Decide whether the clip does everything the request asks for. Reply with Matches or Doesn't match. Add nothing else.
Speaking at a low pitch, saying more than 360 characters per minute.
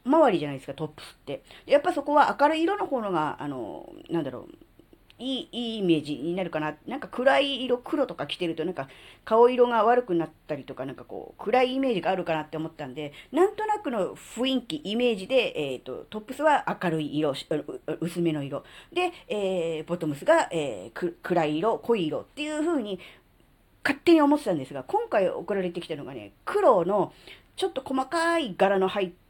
Doesn't match